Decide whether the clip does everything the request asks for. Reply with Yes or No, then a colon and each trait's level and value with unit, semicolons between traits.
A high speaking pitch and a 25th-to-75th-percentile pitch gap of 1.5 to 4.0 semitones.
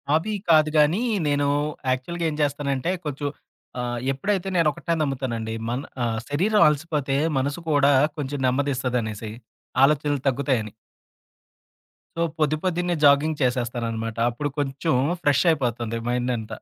No: medium, 140 Hz; average, 3.6 semitones